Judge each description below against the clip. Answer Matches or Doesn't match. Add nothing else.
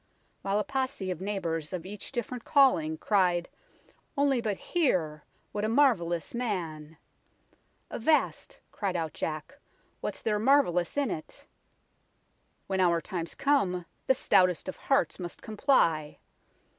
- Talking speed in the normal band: Matches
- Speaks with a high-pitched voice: Matches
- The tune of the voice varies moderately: Doesn't match